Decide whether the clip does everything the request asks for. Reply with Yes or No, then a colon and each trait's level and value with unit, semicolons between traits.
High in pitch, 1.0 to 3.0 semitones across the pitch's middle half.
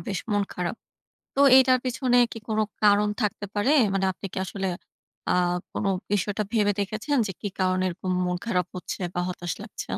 Yes: high, 205 Hz; average, 2.7 semitones